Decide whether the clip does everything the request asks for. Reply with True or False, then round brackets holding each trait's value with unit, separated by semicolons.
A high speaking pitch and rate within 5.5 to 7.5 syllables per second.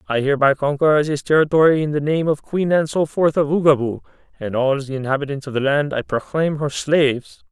False (145 Hz; 5.6 syllables/s)